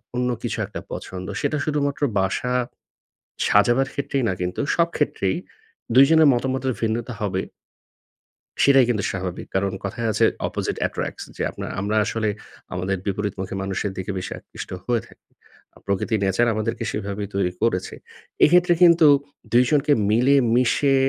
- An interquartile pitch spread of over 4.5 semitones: Yes, wide, 5.6 semitones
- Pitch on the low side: Yes, low, 115 Hz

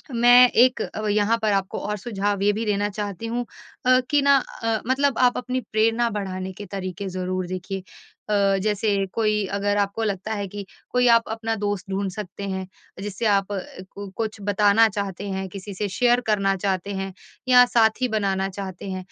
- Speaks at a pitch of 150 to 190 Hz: No, high, 205 Hz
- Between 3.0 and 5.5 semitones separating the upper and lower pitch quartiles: No, narrow, 2.6 semitones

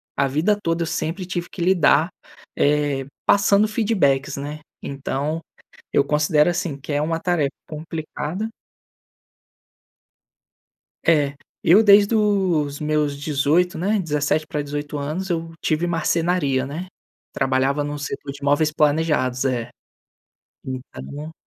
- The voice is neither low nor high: Yes, medium, 155 Hz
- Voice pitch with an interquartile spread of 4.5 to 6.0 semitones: No, average, 3.4 semitones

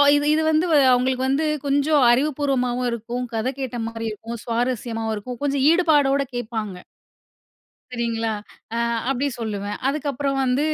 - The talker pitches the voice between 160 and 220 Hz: No, very high, 250 Hz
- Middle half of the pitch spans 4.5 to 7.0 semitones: No, average, 3.5 semitones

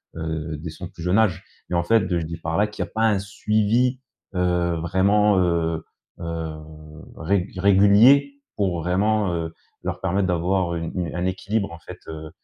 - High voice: No, very low, 90 Hz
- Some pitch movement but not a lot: Yes, average, 3.4 semitones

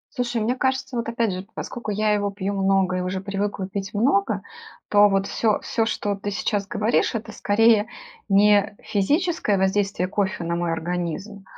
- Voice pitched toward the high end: Yes, high, 205 Hz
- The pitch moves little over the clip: Yes, narrow, 2.1 semitones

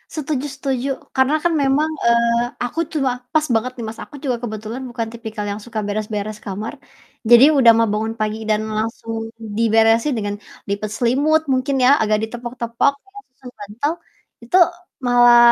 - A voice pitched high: Yes, high, 235 Hz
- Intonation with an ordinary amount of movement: Yes, average, 3.4 semitones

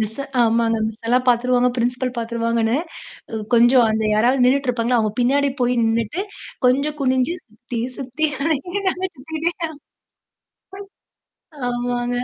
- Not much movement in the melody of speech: Yes, narrow, 2.2 semitones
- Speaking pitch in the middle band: No, high, 245 Hz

